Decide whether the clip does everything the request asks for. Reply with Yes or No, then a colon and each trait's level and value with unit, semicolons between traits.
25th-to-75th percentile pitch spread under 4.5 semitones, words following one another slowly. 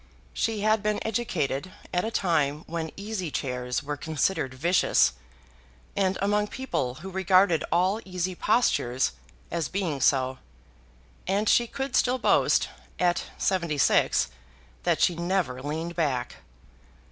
No: wide, 5.4 semitones; slow, 130 wpm